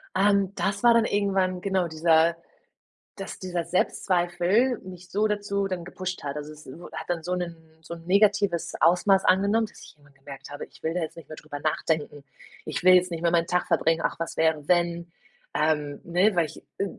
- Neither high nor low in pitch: Yes, medium, 175 Hz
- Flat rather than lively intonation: No, average, 3.2 semitones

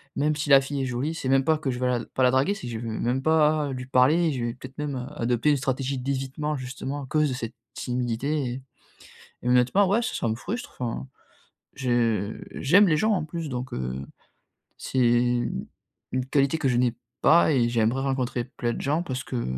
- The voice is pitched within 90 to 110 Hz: No, low, 130 Hz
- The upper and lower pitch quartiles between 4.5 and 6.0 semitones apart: No, average, 3.3 semitones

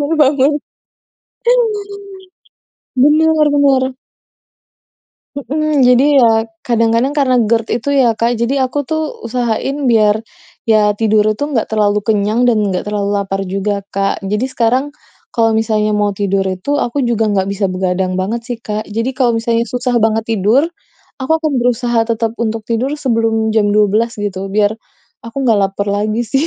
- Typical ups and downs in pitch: Yes, average, 3.3 semitones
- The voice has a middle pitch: No, high, 225 Hz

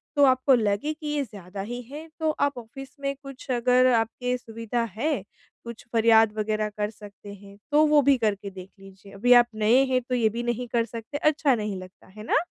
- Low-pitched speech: No, high, 235 Hz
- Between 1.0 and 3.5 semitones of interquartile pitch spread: No, average, 4.1 semitones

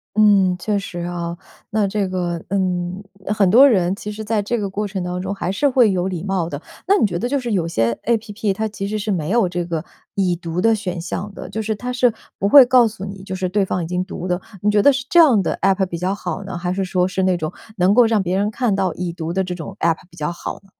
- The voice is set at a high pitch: Yes, high, 195 Hz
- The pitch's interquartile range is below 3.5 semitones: Yes, average, 3.0 semitones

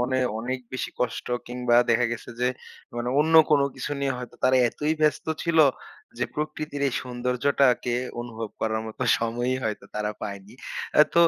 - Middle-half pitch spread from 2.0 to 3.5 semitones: Yes, average, 2.9 semitones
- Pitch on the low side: Yes, low, 125 Hz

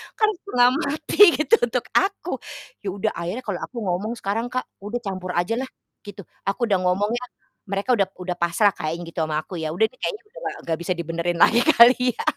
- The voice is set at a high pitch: Yes, high, 200 Hz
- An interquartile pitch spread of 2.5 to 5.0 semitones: No, wide, 5.6 semitones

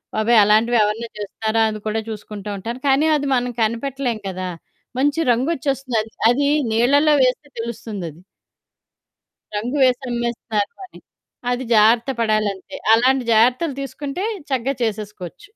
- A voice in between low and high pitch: No, high, 235 Hz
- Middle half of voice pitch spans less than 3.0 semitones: No, average, 3.7 semitones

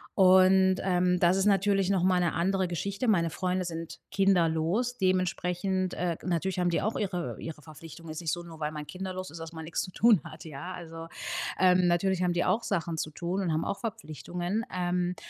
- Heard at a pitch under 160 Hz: No, medium, 180 Hz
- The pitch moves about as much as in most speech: No, narrow, 2.2 semitones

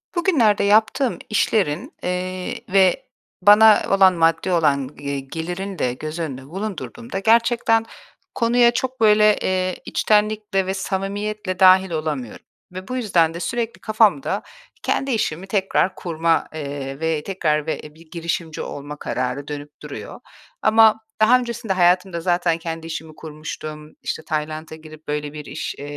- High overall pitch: No, medium, 180 Hz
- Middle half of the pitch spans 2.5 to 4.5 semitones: No, average, 5.3 semitones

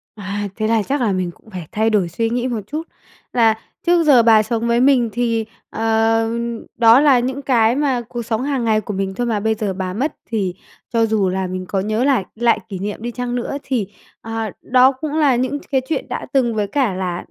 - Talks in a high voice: Yes, high, 225 Hz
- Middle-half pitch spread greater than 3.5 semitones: No, average, 3.2 semitones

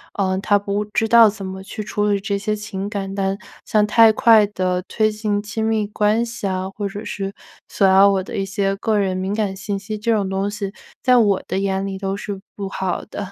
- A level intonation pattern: Yes, narrow, 1.5 semitones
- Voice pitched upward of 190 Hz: Yes, high, 200 Hz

